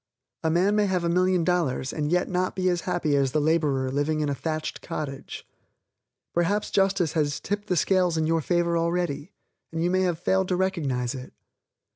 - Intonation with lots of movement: No, average, 3.5 semitones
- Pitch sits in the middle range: Yes, medium, 170 Hz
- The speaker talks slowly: No, average, 190 wpm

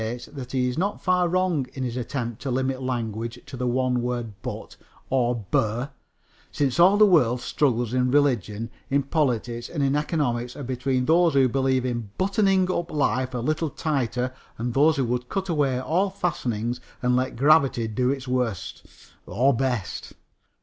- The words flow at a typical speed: Yes, average, 170 wpm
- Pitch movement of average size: Yes, average, 3.3 semitones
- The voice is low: Yes, low, 130 Hz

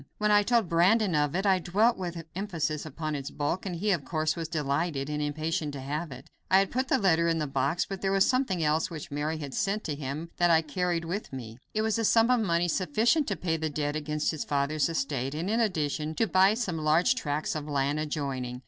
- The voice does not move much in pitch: No, average, 4.5 semitones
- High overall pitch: No, medium, 165 Hz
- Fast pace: Yes, fast, 240 wpm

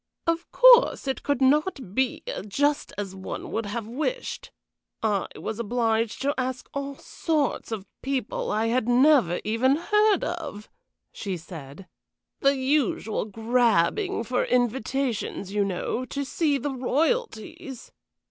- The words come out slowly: Yes, slow, 130 wpm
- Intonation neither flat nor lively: Yes, average, 4.8 semitones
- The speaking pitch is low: No, very high, 255 Hz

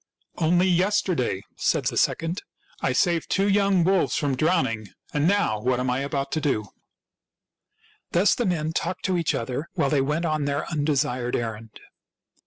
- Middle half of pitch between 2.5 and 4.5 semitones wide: No, wide, 5.6 semitones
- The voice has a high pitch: No, medium, 150 Hz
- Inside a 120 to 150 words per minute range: No, average, 180 wpm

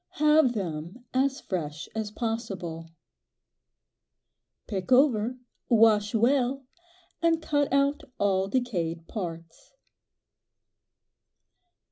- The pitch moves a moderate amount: No, wide, 6.6 semitones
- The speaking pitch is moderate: No, high, 225 Hz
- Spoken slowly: Yes, slow, 80 wpm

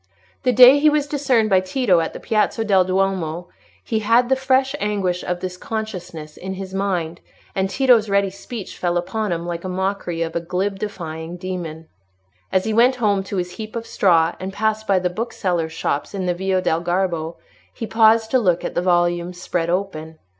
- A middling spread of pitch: Yes, average, 3.8 semitones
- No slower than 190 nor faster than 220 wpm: Yes, average, 195 wpm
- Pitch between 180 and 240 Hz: Yes, high, 190 Hz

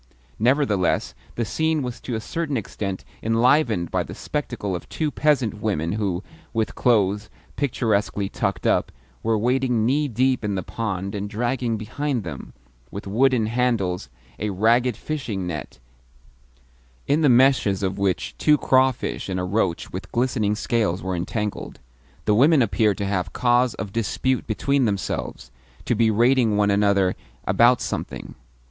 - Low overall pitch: Yes, low, 110 Hz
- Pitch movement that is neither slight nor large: Yes, average, 4.1 semitones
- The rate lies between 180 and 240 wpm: No, average, 150 wpm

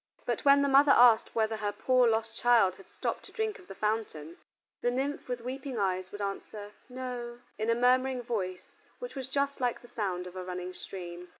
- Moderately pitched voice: No, high, 230 Hz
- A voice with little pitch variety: No, average, 4.8 semitones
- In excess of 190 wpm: Yes, fast, 205 wpm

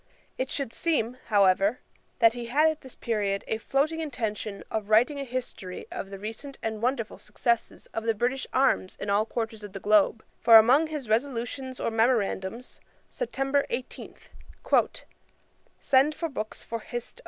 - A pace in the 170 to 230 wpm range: No, average, 160 wpm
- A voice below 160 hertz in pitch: No, high, 235 Hz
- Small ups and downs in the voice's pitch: No, average, 3.9 semitones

